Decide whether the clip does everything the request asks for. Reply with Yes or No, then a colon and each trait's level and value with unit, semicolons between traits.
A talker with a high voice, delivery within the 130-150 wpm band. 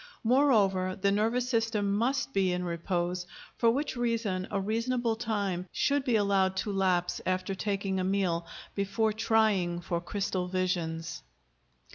Yes: high, 200 Hz; average, 140 wpm